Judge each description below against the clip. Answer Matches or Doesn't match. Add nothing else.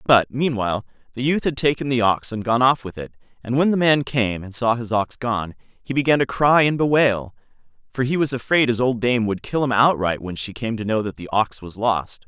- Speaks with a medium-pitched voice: Doesn't match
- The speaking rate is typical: Doesn't match